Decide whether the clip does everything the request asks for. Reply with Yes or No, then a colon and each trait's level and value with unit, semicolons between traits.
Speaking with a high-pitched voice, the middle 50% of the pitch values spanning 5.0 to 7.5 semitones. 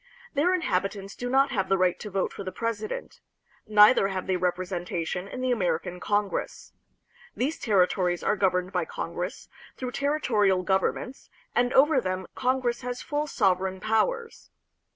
Yes: high, 200 Hz; average, 5.3 semitones